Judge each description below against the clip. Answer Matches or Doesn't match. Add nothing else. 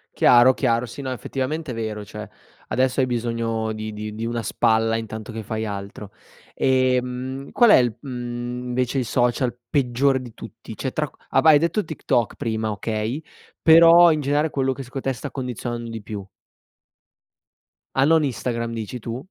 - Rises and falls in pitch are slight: Doesn't match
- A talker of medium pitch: Doesn't match